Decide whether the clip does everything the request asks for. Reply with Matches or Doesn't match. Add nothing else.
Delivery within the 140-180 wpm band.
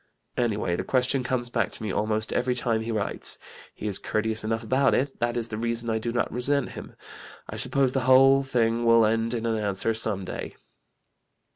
Doesn't match